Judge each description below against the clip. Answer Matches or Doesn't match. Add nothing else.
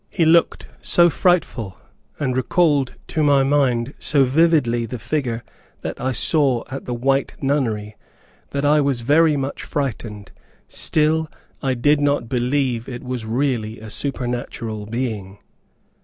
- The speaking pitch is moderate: Doesn't match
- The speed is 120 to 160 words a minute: Matches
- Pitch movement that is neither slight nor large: Matches